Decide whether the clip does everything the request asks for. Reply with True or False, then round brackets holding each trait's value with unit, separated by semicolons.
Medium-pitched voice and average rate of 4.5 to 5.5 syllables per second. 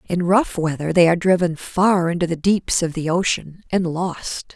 True (175 Hz; 4.7 syllables/s)